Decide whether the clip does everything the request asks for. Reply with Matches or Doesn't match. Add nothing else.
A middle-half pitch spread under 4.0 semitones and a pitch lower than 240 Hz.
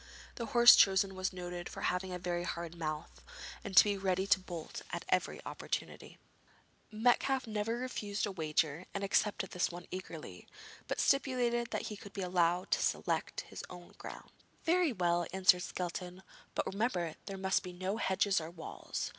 Matches